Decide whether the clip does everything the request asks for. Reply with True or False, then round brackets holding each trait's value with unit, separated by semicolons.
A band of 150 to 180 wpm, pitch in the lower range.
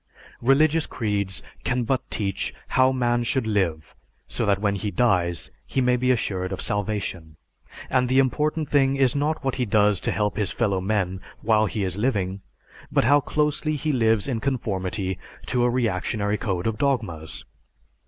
True (170 wpm; 110 Hz)